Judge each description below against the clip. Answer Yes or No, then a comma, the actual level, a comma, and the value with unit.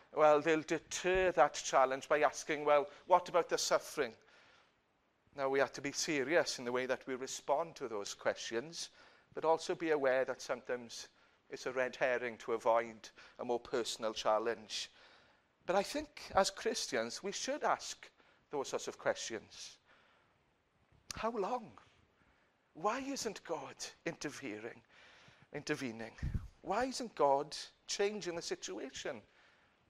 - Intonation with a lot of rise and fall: Yes, wide, 7.2 semitones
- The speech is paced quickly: No, slow, 135 wpm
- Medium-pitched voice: Yes, medium, 155 Hz